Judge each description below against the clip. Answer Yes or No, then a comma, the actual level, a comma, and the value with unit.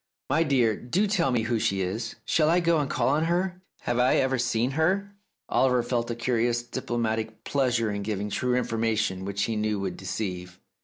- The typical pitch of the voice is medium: No, low, 120 Hz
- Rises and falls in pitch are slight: No, average, 4.0 semitones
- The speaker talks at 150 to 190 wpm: No, average, 200 wpm